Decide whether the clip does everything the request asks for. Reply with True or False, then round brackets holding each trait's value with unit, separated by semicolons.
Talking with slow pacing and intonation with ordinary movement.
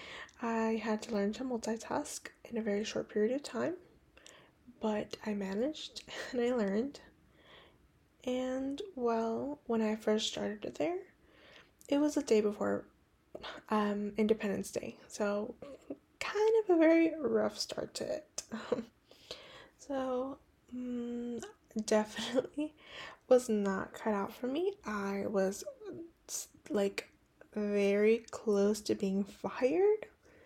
True (120 wpm; 4.7 semitones)